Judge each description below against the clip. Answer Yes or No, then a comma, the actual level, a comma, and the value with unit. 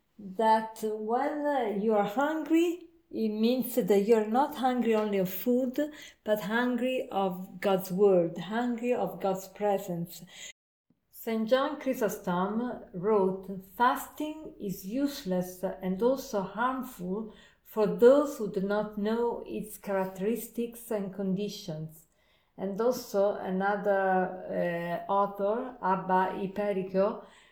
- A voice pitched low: No, high, 210 Hz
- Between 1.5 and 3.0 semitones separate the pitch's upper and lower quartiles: No, average, 4.1 semitones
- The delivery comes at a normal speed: No, slow, 110 wpm